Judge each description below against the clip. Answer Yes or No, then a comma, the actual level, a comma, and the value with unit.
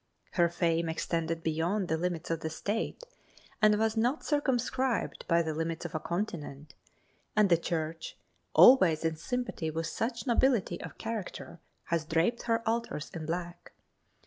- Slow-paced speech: No, average, 150 wpm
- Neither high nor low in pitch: Yes, medium, 170 Hz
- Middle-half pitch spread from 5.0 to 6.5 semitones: Yes, wide, 5.6 semitones